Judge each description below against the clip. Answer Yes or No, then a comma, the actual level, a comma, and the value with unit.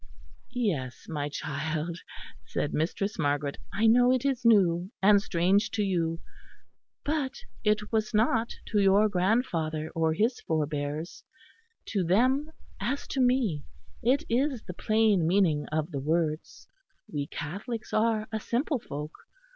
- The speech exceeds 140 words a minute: No, slow, 135 wpm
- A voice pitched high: Yes, high, 195 Hz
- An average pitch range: No, wide, 6.3 semitones